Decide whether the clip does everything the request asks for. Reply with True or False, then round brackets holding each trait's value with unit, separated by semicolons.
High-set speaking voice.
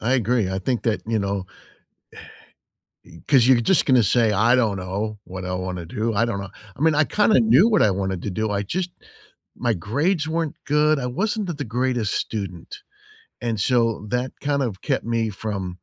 False (115 Hz)